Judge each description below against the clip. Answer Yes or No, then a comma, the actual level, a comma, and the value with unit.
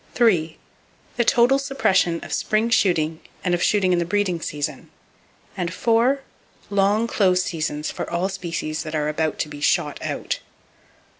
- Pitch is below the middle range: No, medium, 180 Hz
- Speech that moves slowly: No, average, 145 wpm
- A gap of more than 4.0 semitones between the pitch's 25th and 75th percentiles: Yes, average, 5.1 semitones